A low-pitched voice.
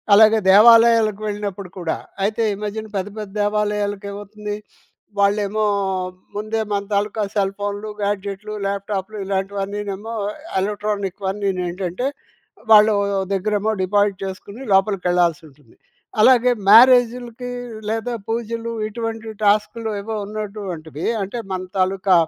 No: high, 205 Hz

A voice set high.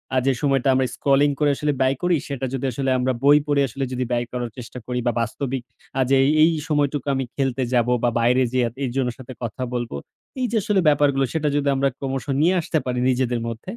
No: low, 135 Hz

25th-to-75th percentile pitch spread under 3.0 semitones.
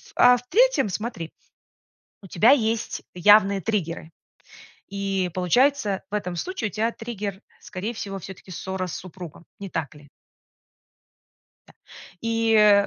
No: average, 3.6 semitones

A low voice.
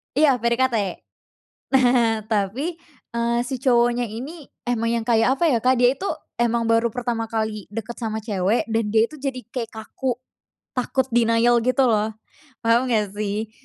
No: high, 235 Hz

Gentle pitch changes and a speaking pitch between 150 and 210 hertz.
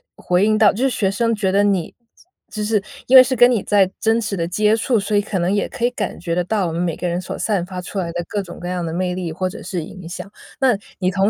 No: average, 3.2 semitones; high, 195 Hz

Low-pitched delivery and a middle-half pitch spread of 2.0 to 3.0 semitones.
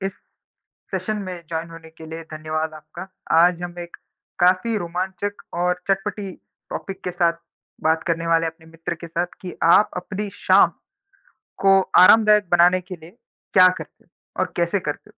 No: medium, 175 Hz; narrow, 2.5 semitones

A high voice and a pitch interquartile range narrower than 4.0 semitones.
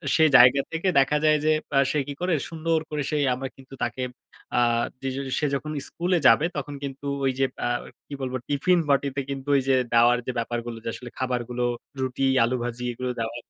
No: low, 135 Hz; average, 3.4 semitones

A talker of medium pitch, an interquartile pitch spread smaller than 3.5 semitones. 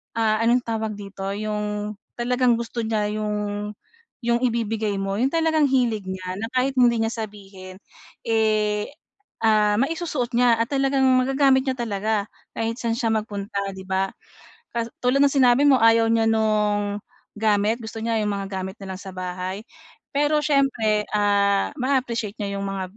No: high, 220 Hz; average, 3.1 semitones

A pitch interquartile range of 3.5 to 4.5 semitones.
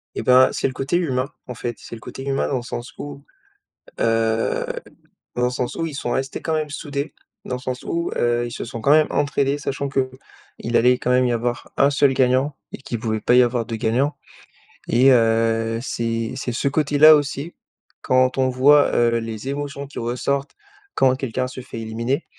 No: average, 2.8 semitones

